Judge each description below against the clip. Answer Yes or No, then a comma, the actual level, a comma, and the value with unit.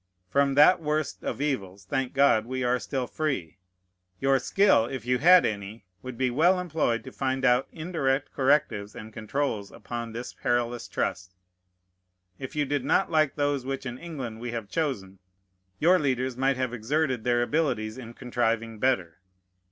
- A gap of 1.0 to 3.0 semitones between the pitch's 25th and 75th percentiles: No, average, 3.7 semitones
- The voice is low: Yes, low, 130 Hz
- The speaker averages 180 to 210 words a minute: No, average, 165 wpm